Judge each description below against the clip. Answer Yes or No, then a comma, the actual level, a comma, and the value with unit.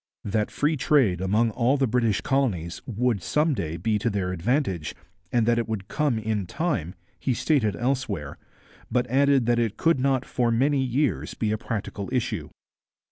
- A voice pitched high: No, low, 115 Hz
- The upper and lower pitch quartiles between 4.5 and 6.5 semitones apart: Yes, average, 4.8 semitones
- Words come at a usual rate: Yes, average, 175 wpm